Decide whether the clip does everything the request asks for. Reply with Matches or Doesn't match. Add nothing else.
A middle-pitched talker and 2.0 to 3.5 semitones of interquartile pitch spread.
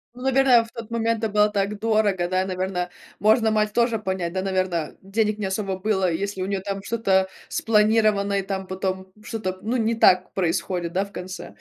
Doesn't match